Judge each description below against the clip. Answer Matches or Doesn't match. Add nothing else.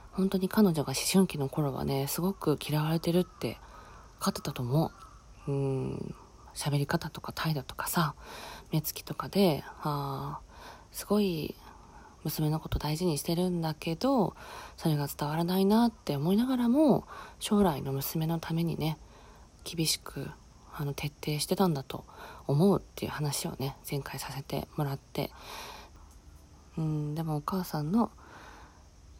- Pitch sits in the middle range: Matches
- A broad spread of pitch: Doesn't match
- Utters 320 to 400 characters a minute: Doesn't match